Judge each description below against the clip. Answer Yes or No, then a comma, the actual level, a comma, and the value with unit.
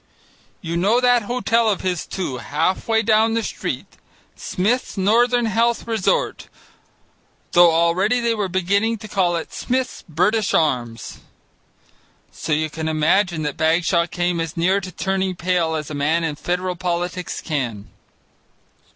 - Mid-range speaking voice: Yes, medium, 180 Hz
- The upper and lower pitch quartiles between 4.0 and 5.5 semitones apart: Yes, average, 5.1 semitones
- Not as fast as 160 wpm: Yes, average, 145 wpm